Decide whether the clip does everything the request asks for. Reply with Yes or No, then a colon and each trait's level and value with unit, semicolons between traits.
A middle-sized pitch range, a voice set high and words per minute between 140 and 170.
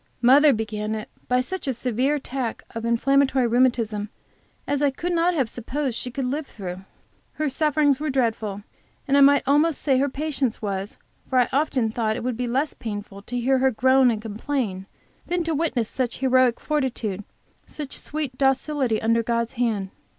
No: average, 3.8 semitones; very high, 255 Hz; average, 180 wpm